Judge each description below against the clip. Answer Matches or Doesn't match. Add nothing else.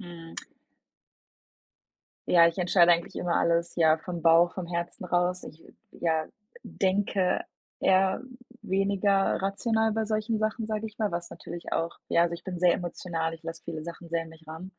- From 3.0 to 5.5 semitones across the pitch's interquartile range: Doesn't match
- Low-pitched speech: Doesn't match